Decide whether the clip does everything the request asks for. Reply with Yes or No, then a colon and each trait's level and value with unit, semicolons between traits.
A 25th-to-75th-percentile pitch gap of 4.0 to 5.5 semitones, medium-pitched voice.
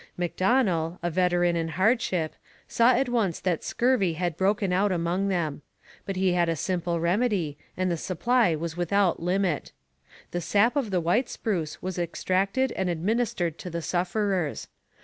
No: average, 3.1 semitones; medium, 180 Hz